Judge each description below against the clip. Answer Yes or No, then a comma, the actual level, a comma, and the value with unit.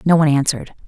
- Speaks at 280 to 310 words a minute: No, fast, 205 wpm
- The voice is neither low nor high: Yes, medium, 150 Hz